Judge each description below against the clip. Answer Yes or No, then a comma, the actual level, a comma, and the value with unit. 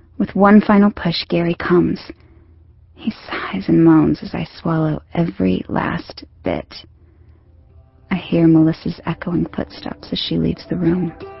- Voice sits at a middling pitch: Yes, medium, 165 Hz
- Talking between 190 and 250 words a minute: No, slow, 135 wpm